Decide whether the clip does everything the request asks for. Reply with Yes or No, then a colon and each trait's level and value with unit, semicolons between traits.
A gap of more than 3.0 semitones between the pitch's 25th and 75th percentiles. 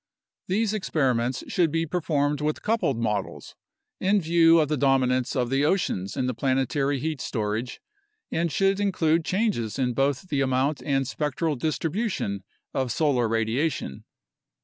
Yes: average, 4.5 semitones